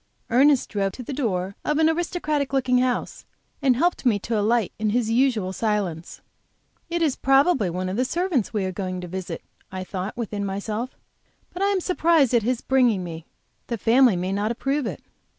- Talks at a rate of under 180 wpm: No, average, 190 wpm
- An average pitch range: No, wide, 5.7 semitones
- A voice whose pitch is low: No, high, 235 Hz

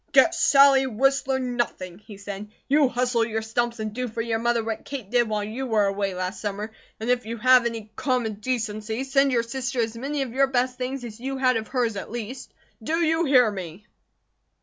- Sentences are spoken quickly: Yes, fast, 210 wpm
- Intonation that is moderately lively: Yes, average, 3.1 semitones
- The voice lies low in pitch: No, high, 235 Hz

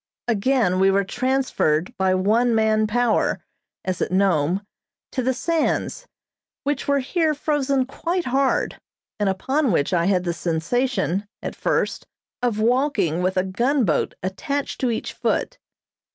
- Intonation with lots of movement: Yes, wide, 6.2 semitones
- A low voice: No, high, 225 Hz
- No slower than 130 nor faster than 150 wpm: Yes, average, 140 wpm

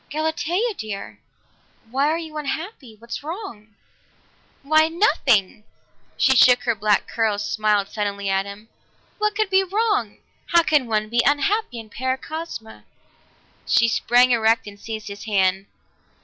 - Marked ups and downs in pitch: Yes, wide, 6.9 semitones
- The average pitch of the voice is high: Yes, high, 240 Hz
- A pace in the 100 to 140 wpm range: Yes, slow, 135 wpm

